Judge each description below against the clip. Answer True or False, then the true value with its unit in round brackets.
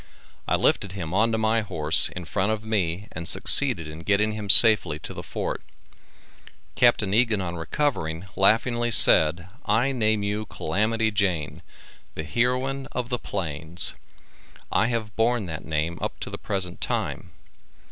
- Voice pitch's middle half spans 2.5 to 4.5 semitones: False (4.9 semitones)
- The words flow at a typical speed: True (150 wpm)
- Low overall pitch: True (105 Hz)